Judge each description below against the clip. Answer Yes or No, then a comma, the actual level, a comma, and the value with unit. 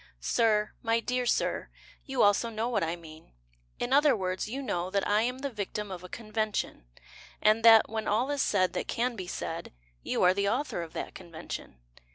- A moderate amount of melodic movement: Yes, average, 4.3 semitones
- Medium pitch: No, high, 215 Hz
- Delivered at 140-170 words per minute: No, average, 200 wpm